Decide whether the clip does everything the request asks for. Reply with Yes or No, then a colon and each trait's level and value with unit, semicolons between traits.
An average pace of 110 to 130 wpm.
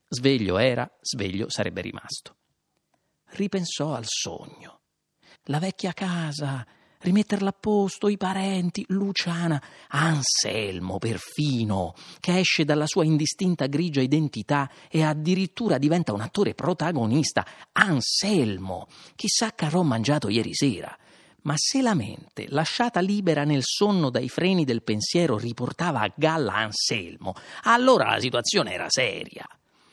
Yes: average, 120 wpm